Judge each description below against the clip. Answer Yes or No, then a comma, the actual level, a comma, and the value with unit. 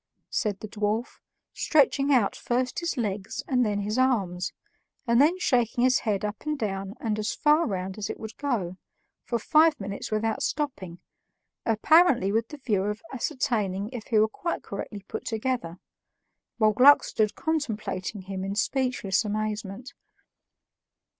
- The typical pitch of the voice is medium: No, high, 220 Hz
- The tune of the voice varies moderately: Yes, average, 4.2 semitones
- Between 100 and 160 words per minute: Yes, average, 155 wpm